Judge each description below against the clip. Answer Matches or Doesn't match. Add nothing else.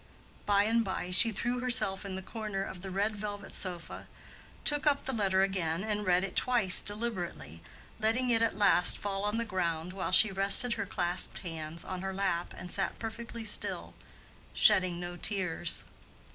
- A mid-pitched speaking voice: Doesn't match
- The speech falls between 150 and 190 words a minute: Matches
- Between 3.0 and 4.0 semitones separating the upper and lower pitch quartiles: Matches